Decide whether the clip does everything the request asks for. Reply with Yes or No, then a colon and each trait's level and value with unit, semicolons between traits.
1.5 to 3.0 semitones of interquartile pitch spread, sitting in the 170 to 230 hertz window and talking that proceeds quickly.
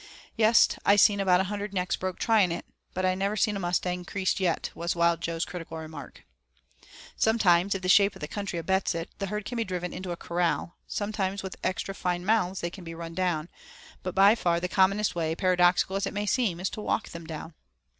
Yes: narrow, 2.6 semitones; medium, 185 Hz; fast, 220 wpm